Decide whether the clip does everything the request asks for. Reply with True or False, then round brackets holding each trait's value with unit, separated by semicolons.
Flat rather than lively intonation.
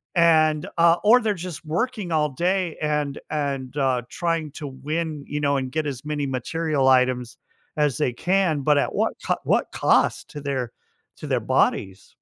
False (3.7 semitones)